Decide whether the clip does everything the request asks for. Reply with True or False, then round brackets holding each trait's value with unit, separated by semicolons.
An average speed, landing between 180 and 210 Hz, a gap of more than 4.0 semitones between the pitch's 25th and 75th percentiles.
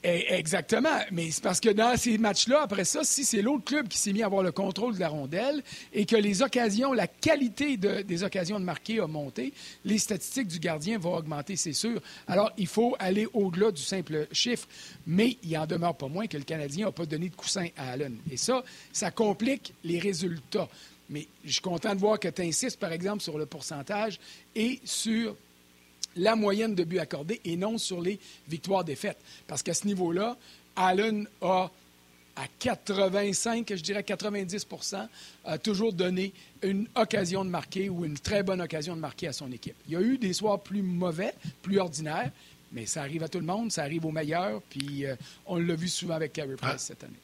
True (205 wpm; 190 Hz; 4.5 semitones)